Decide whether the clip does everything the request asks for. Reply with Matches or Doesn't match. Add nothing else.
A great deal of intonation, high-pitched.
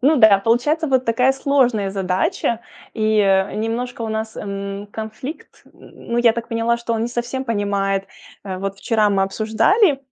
Doesn't match